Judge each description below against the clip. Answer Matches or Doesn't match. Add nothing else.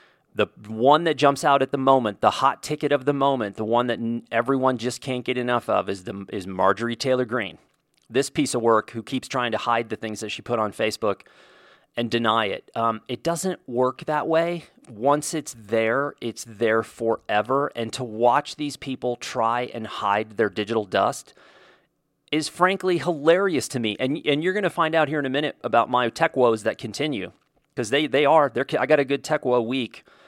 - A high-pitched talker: Doesn't match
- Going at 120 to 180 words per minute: Doesn't match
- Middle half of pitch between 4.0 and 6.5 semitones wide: Matches